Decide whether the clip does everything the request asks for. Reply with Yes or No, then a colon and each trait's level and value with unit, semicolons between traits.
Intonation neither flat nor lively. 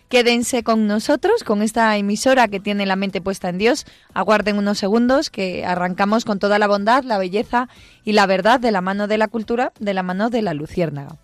Yes: average, 3.5 semitones